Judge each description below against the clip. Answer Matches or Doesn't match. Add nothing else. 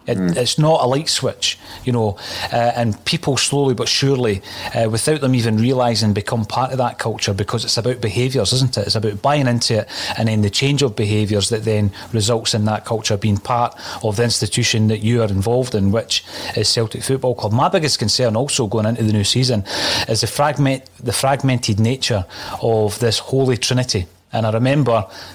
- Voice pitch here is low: Matches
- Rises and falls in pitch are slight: Doesn't match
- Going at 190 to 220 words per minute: Matches